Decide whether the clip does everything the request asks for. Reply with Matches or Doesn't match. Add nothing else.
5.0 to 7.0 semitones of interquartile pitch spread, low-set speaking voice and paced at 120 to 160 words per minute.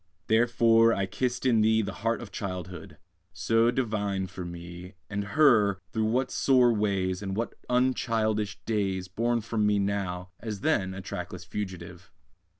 Doesn't match